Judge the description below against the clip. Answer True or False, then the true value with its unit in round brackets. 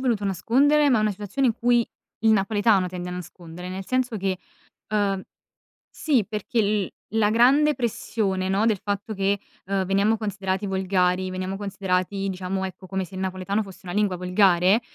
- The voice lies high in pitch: True (195 Hz)